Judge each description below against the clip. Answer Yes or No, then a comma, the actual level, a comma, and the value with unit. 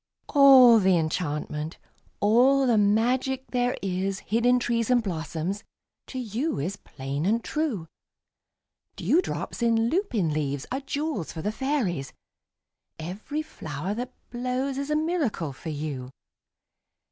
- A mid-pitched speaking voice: No, high, 225 Hz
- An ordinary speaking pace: No, slow, 130 wpm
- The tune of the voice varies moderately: No, wide, 7.8 semitones